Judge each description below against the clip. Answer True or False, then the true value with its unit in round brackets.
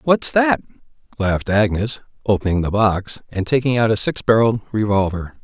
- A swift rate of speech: False (155 wpm)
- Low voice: True (110 Hz)